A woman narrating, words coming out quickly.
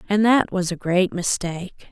No: female; average, 190 wpm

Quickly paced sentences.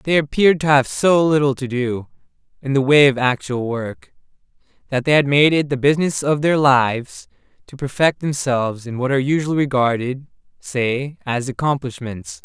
No: average, 170 wpm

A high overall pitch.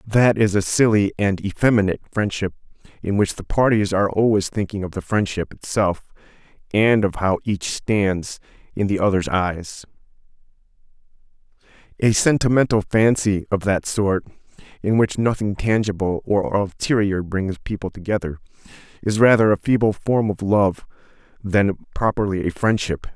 No: low, 100 Hz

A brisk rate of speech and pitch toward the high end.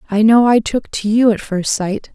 Yes: fast, 250 wpm; high, 215 Hz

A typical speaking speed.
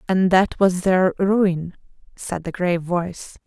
Yes: average, 155 wpm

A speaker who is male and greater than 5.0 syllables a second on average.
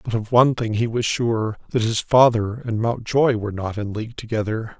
Yes: male; 5.3 syllables/s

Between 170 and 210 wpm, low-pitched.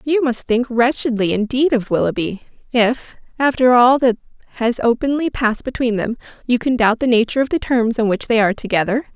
No: average, 190 wpm; high, 240 Hz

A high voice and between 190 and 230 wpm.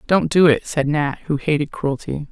No: medium, 150 Hz; fast, 205 wpm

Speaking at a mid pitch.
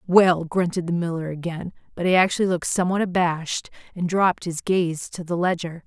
Yes: medium, 175 Hz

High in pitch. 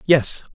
No: medium, 150 Hz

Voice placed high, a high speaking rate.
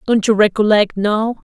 No: high, 215 Hz; average, 160 wpm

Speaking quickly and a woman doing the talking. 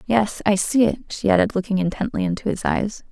Yes: fast, 210 wpm; female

